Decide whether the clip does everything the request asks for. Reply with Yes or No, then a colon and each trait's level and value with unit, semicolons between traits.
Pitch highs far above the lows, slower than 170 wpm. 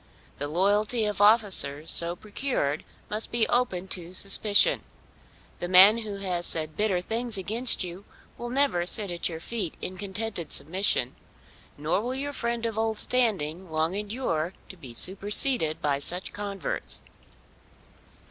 No: average, 4.6 semitones; average, 145 wpm